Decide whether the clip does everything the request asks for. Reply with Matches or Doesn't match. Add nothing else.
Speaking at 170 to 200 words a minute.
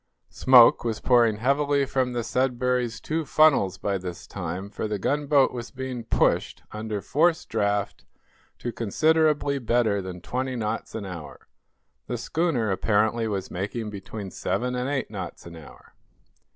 Doesn't match